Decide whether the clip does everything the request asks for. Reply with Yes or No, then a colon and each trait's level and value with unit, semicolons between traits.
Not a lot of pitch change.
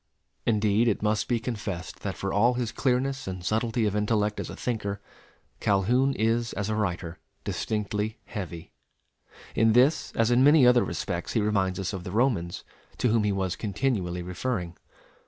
No: average, 3.7 semitones